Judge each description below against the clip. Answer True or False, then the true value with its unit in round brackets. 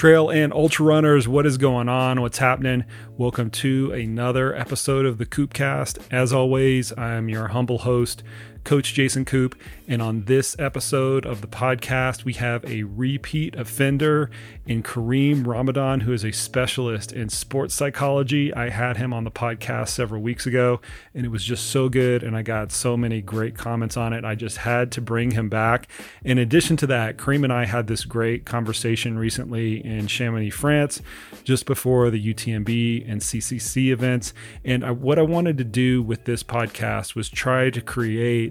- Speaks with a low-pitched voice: True (125 Hz)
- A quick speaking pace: False (180 wpm)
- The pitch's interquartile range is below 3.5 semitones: True (2.5 semitones)